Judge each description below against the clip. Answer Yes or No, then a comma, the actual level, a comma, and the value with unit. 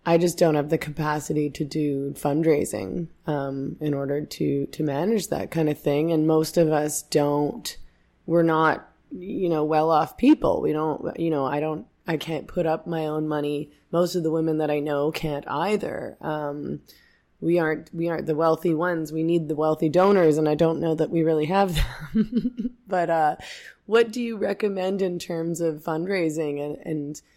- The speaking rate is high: No, average, 190 wpm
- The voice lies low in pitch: No, medium, 160 Hz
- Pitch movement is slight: Yes, narrow, 2.1 semitones